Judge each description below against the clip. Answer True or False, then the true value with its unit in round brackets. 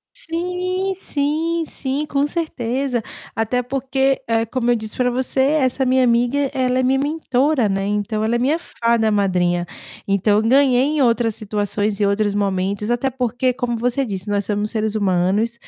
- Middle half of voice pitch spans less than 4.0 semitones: False (4.3 semitones)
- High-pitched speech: True (240 Hz)